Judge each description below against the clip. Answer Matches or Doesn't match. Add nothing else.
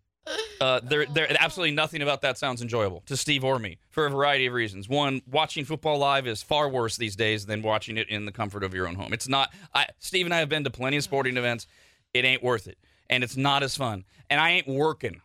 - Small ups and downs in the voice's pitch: Doesn't match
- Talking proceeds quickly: Matches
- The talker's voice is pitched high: Doesn't match